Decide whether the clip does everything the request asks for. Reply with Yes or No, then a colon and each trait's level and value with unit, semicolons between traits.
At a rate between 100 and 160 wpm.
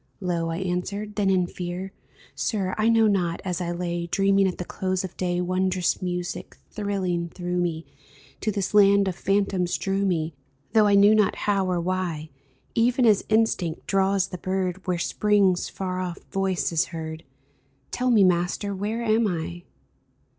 No: average, 170 wpm